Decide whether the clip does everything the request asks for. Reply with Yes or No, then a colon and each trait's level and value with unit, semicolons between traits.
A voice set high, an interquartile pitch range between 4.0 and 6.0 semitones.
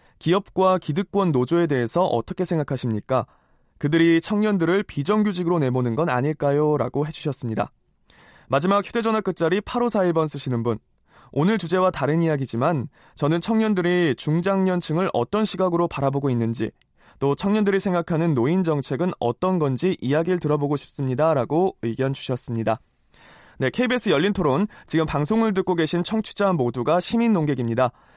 No: medium, 165 Hz; wide, 5.6 semitones